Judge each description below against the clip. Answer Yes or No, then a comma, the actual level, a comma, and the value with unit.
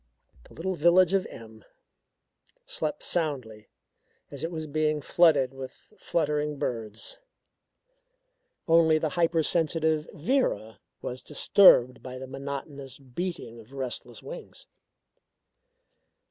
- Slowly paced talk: Yes, slow, 105 wpm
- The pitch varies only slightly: No, average, 4.2 semitones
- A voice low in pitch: No, medium, 150 Hz